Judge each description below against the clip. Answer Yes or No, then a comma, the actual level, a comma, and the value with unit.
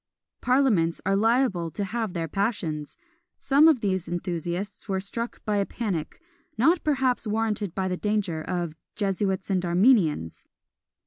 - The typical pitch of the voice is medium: No, high, 195 Hz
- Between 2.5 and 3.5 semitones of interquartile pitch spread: No, average, 4.4 semitones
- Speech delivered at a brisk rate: No, average, 140 wpm